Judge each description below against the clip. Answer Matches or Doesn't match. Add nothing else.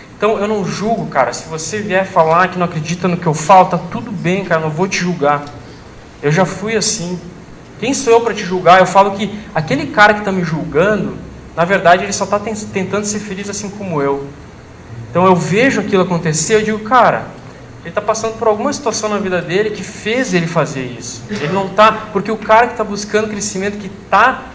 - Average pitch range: Matches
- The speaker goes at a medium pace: Doesn't match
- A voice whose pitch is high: Matches